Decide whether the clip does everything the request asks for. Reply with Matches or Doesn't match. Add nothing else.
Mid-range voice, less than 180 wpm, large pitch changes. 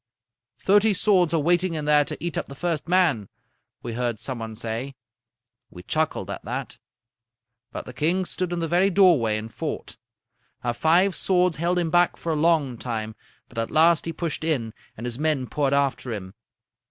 Doesn't match